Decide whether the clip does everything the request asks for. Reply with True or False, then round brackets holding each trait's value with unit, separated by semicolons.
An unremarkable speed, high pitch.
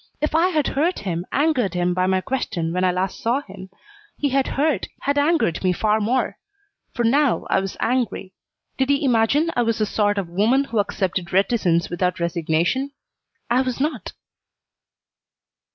True (170 wpm; 225 Hz)